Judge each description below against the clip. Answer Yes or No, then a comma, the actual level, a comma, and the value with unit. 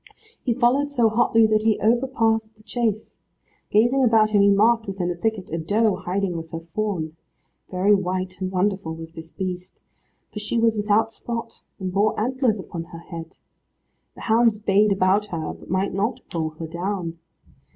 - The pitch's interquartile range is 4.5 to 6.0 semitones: No, average, 3.6 semitones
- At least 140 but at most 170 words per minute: No, average, 180 wpm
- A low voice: No, high, 205 Hz